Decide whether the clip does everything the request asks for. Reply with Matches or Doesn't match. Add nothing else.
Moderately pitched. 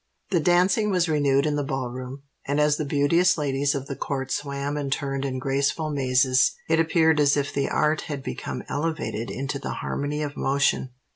Matches